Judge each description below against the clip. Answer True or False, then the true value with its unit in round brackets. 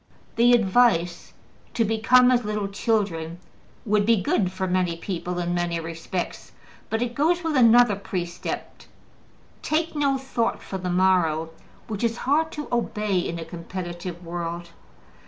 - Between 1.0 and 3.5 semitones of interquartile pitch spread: False (5.5 semitones)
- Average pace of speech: True (145 wpm)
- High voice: True (195 Hz)